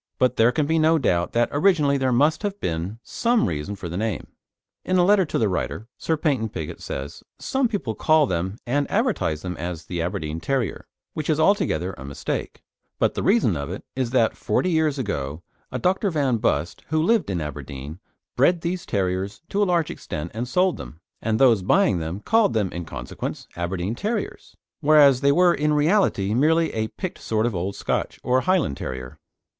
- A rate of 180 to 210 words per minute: Yes, average, 195 wpm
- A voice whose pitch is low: Yes, low, 120 Hz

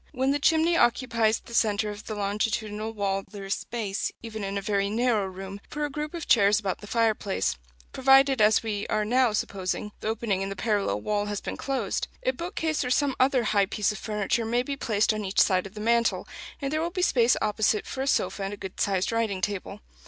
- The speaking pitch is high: Yes, high, 215 Hz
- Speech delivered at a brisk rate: Yes, fast, 225 wpm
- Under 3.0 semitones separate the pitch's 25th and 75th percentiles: No, average, 3.7 semitones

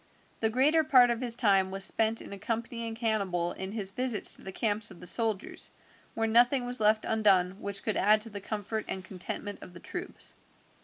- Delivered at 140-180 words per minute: No, average, 200 wpm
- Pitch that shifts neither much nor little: Yes, average, 3.0 semitones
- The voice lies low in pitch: No, high, 215 Hz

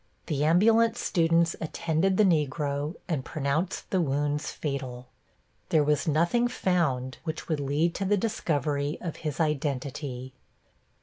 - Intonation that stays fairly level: No, average, 3.3 semitones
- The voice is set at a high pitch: No, medium, 155 Hz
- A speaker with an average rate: No, slow, 130 wpm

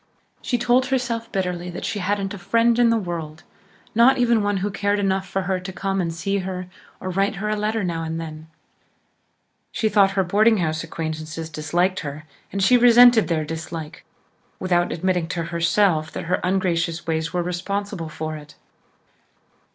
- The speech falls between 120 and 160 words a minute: No, average, 175 wpm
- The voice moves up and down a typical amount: Yes, average, 3.8 semitones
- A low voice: No, medium, 185 Hz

